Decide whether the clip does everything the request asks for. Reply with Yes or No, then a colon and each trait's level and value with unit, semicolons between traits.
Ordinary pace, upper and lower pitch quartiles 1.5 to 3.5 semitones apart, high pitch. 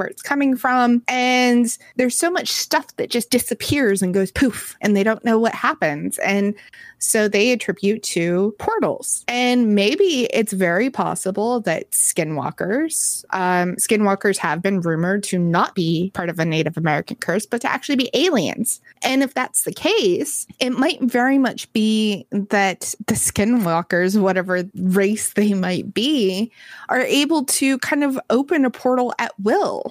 No: average, 165 wpm; average, 4.9 semitones; high, 220 Hz